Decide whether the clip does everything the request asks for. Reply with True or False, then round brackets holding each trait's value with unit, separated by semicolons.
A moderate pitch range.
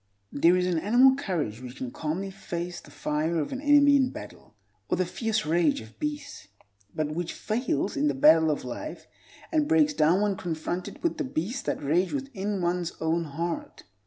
False (7.8 semitones)